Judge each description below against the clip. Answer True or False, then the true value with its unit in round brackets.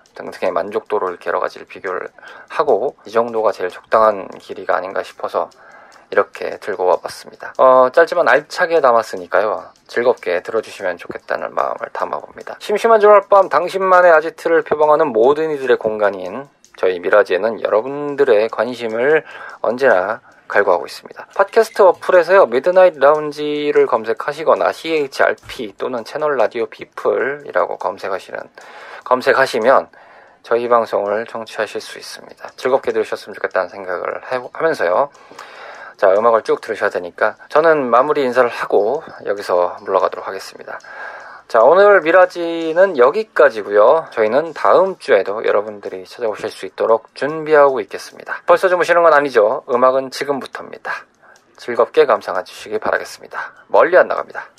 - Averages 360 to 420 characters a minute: True (365 characters per minute)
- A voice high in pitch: True (210 Hz)